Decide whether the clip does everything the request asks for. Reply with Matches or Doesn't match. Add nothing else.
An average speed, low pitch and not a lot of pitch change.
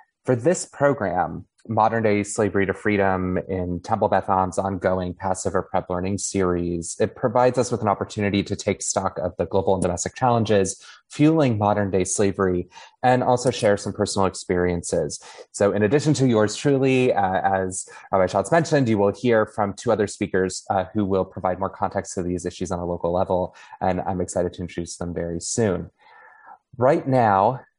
Doesn't match